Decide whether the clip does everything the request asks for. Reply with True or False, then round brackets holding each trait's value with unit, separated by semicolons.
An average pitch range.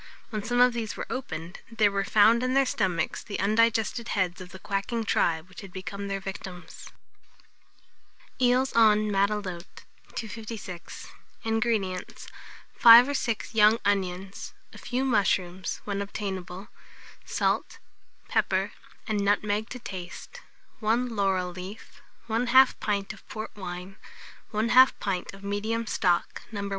True (3.2 semitones)